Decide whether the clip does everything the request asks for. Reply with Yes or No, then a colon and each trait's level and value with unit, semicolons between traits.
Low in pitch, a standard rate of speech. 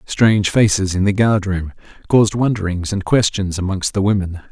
Yes: low, 100 Hz; average, 175 wpm